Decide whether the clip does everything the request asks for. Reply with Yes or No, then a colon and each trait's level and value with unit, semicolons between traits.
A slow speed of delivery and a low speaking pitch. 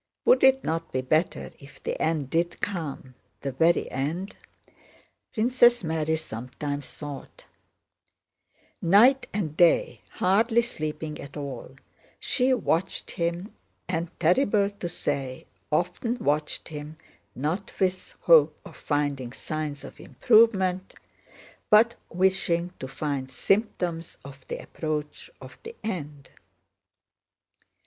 No: slow, 115 wpm; medium, 165 Hz